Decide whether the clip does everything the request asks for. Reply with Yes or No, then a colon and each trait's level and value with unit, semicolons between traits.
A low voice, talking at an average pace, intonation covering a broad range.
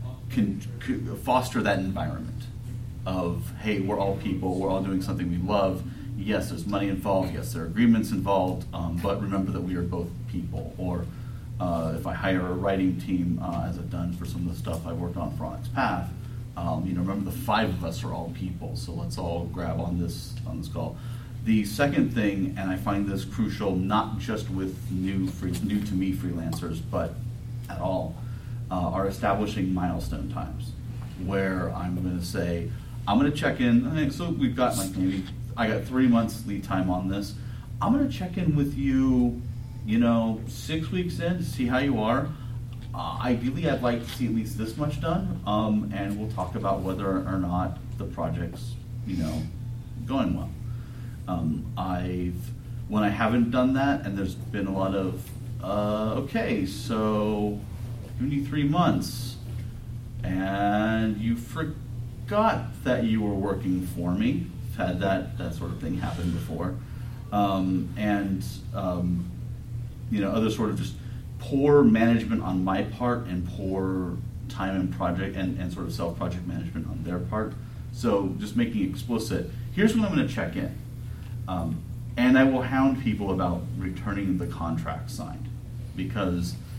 No: low, 110 Hz; average, 175 wpm; average, 4.2 semitones